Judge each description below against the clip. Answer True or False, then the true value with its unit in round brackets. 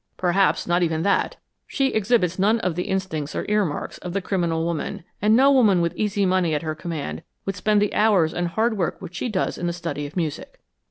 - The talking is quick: True (220 wpm)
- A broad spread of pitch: False (3.7 semitones)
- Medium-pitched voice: True (180 Hz)